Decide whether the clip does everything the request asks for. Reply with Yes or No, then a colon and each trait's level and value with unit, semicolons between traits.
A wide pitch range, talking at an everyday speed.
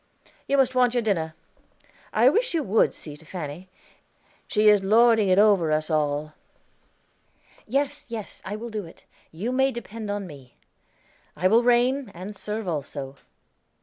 Yes: wide, 6.5 semitones; average, 155 wpm